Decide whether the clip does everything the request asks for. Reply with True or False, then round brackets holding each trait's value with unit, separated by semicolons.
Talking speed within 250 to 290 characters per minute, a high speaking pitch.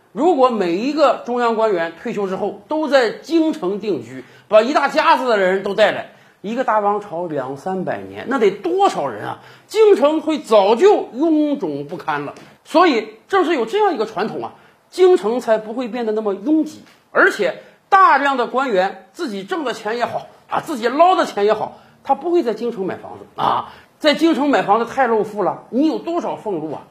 True (280 characters per minute; 245 Hz)